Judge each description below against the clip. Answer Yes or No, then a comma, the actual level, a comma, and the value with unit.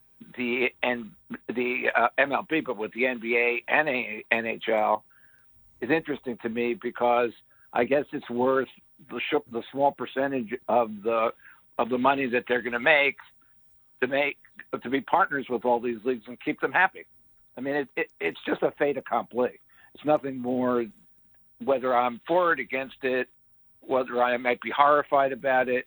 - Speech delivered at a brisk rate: No, average, 165 wpm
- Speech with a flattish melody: Yes, narrow, 2.3 semitones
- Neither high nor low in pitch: No, low, 125 Hz